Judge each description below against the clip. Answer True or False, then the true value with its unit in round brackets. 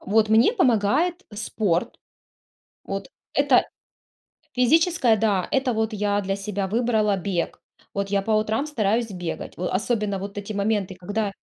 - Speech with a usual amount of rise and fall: False (2.3 semitones)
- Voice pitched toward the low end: False (210 Hz)